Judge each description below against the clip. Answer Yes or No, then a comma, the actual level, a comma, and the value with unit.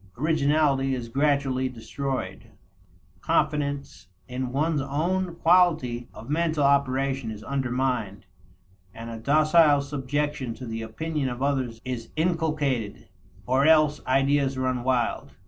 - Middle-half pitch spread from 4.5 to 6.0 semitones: No, average, 3.0 semitones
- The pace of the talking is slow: Yes, slow, 115 wpm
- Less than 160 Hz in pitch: Yes, low, 135 Hz